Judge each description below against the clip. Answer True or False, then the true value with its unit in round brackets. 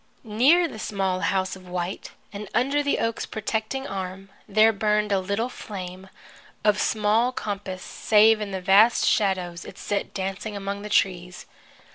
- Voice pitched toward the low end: False (205 Hz)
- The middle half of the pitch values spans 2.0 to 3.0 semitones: True (2.5 semitones)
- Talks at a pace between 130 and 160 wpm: True (155 wpm)